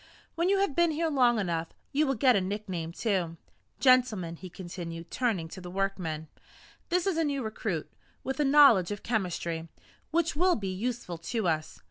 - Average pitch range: No, wide, 8.1 semitones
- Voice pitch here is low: No, high, 210 Hz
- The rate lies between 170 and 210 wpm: Yes, average, 180 wpm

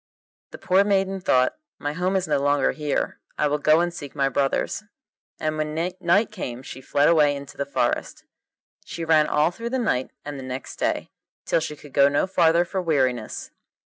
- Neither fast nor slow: Yes, average, 195 wpm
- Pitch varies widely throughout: No, average, 3.8 semitones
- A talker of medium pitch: Yes, medium, 150 Hz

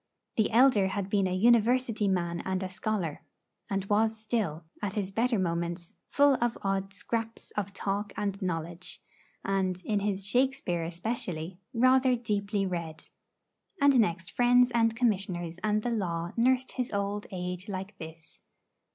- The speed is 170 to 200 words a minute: No, average, 150 wpm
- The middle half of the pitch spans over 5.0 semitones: No, average, 3.9 semitones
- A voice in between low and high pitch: No, high, 200 Hz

